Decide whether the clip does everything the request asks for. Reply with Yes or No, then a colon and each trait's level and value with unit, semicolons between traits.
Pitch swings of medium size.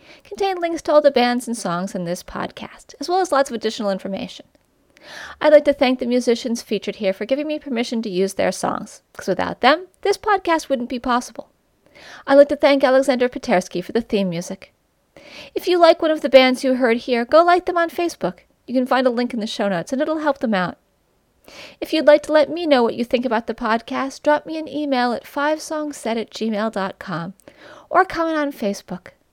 Yes: average, 5.0 semitones